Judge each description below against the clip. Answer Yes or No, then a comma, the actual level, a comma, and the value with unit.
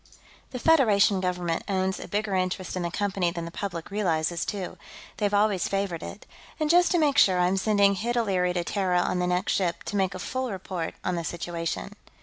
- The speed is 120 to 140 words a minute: No, fast, 205 wpm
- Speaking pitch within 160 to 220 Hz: Yes, high, 190 Hz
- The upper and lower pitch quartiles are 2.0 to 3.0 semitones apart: Yes, narrow, 2.5 semitones